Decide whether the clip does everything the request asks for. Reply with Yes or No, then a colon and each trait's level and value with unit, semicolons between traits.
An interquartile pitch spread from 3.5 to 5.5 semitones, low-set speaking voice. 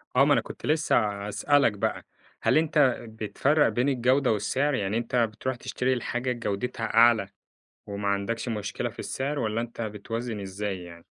Yes: average, 3.9 semitones; low, 115 Hz